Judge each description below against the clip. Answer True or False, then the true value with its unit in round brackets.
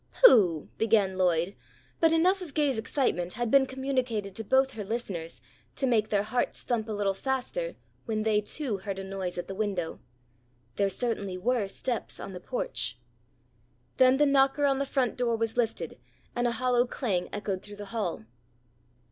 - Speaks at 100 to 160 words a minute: False (175 wpm)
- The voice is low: False (225 Hz)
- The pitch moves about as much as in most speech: True (5.0 semitones)